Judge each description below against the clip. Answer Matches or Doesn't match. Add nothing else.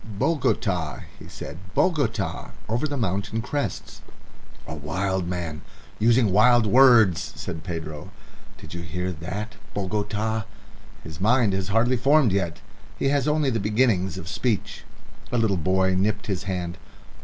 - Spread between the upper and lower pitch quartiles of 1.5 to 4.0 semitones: Doesn't match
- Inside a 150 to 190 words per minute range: Doesn't match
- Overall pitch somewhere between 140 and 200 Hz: Doesn't match